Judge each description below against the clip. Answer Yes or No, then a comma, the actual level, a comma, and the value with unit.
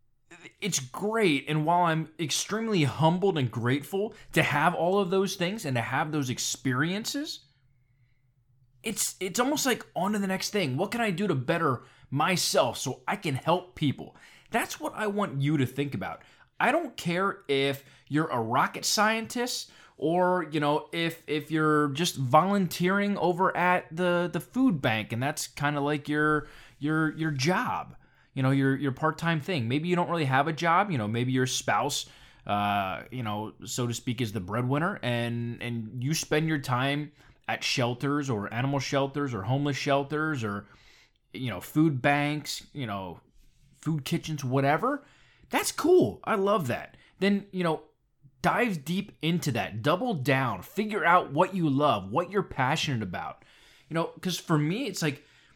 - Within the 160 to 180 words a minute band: Yes, average, 175 wpm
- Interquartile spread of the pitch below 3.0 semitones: No, average, 5.2 semitones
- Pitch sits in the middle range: Yes, medium, 150 Hz